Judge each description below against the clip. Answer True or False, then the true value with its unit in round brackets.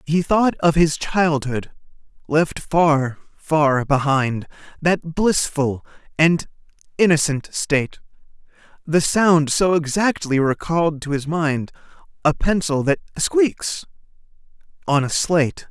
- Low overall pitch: False (155 Hz)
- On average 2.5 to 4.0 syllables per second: True (3.7 syllables/s)